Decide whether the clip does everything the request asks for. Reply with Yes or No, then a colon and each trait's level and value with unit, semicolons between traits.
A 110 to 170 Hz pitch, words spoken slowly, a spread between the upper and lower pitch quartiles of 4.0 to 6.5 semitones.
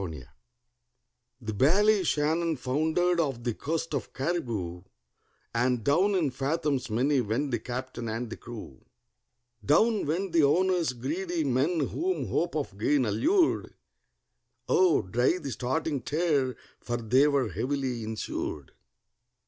Yes: medium, 140 Hz; slow, 120 wpm; wide, 5.6 semitones